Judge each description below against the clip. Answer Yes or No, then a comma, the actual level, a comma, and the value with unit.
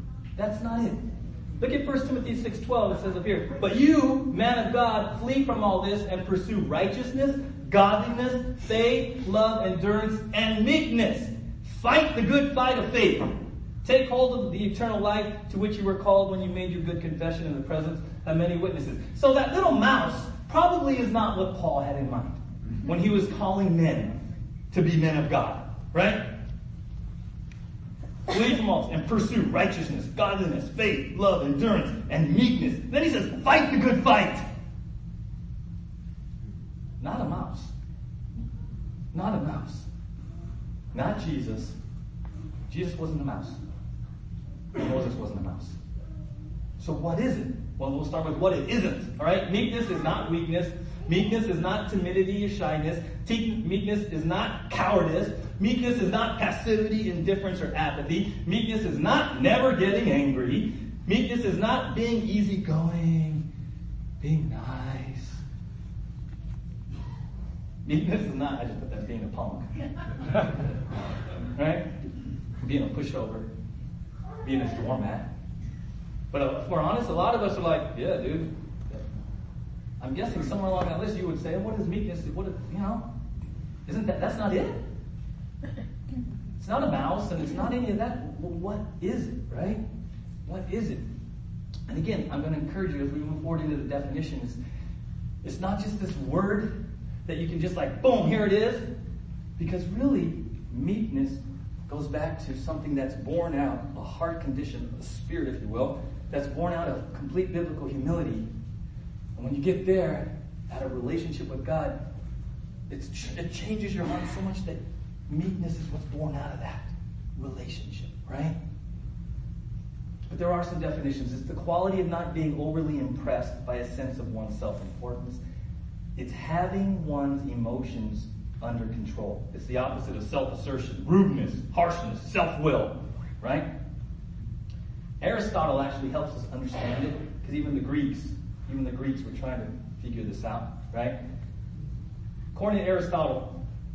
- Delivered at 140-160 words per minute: Yes, average, 155 wpm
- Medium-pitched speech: Yes, medium, 165 Hz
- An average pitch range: No, wide, 7.2 semitones